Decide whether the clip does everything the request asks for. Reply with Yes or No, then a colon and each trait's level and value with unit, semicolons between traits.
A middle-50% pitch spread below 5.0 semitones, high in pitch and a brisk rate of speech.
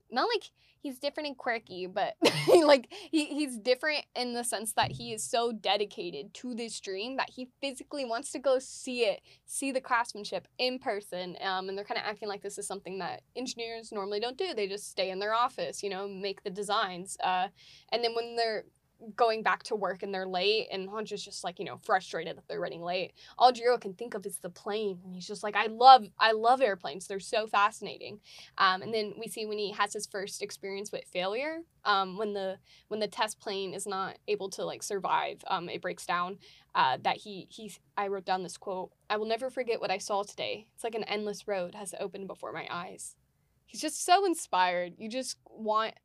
Yes: average, 3.6 semitones; high, 210 Hz; fast, 220 wpm